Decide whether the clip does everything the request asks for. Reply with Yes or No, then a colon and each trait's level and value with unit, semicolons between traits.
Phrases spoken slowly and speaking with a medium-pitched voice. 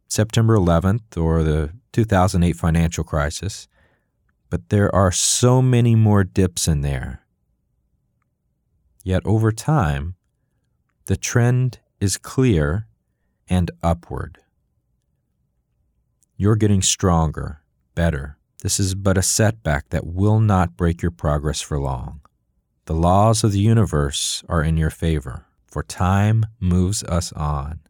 No: slow, 120 wpm; very low, 90 Hz